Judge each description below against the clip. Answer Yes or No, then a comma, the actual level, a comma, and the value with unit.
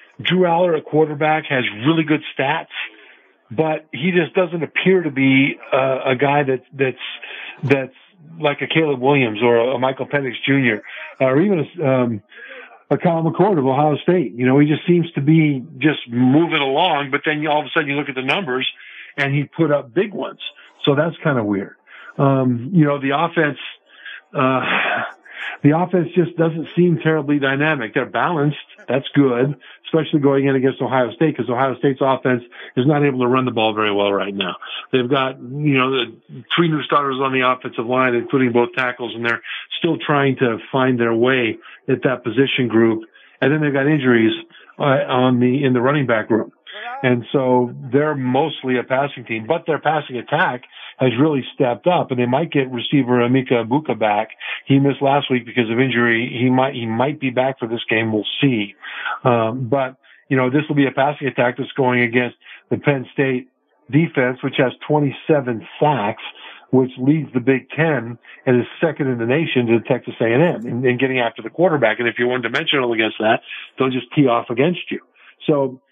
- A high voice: No, low, 135 Hz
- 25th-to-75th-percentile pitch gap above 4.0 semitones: No, average, 3.1 semitones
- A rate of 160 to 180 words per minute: No, average, 195 wpm